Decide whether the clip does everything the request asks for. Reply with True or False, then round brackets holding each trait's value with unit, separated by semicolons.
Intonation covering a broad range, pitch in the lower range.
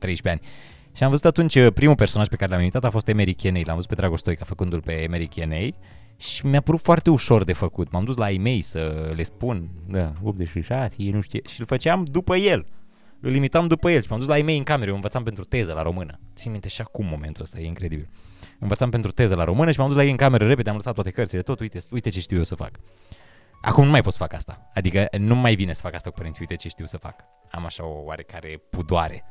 True (5.9 semitones; 100 Hz)